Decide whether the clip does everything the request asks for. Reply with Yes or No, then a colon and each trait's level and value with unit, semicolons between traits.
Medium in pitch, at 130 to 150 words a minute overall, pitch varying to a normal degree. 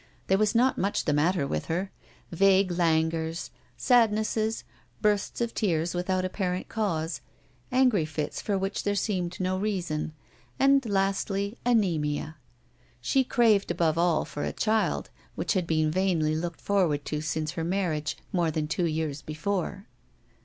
Yes: medium, 180 Hz; average, 145 wpm; average, 4.2 semitones